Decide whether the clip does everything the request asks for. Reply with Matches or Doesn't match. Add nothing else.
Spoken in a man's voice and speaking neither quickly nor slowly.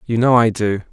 Doesn't match